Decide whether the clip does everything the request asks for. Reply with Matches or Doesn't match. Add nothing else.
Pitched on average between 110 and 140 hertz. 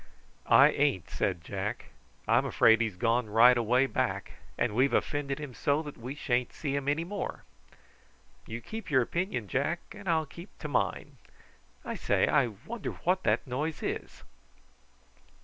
Matches